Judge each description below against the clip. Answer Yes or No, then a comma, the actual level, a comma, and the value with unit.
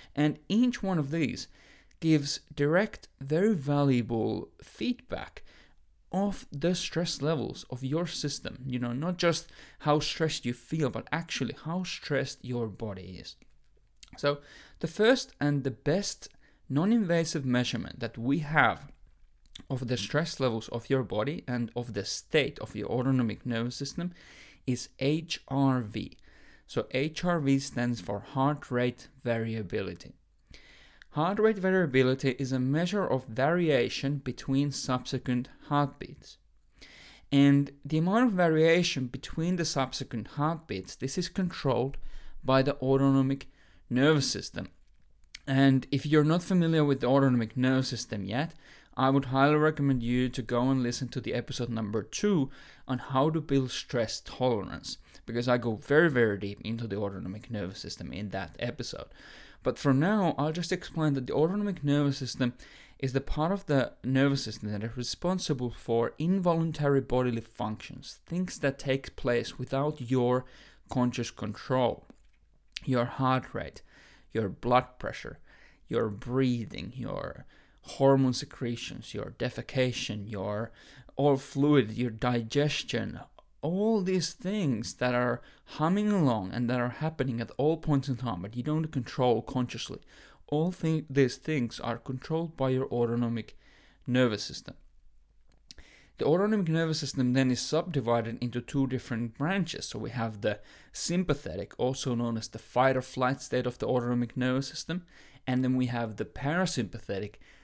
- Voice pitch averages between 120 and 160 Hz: Yes, low, 135 Hz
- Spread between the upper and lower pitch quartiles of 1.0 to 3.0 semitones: No, average, 4.0 semitones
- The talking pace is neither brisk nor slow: Yes, average, 145 wpm